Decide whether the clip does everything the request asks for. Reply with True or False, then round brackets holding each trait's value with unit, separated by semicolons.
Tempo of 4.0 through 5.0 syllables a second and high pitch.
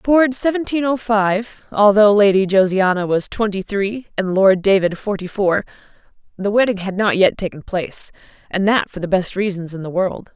True (4.9 syllables/s; 200 Hz)